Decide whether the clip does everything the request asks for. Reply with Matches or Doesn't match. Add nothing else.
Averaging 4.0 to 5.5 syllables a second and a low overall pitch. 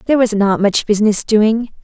Doesn't match